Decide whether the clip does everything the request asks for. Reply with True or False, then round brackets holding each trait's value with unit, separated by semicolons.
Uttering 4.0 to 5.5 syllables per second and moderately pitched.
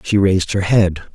False (5.4 syllables/s; 95 Hz)